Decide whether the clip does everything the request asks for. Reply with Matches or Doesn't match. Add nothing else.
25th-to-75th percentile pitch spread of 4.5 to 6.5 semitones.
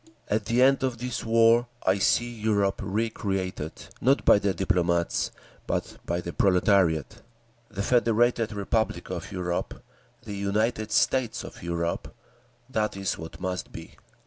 Doesn't match